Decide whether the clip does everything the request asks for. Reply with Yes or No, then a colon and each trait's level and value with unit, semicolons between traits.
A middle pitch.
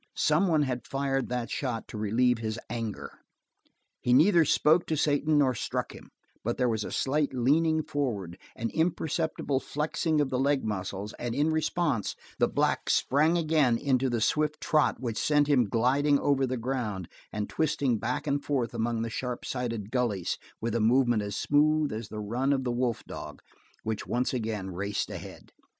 No: low, 125 Hz